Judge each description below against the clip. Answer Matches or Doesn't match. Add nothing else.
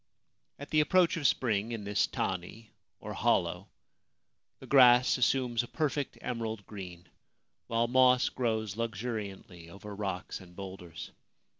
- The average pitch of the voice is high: Doesn't match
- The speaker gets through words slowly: Matches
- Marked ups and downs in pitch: Doesn't match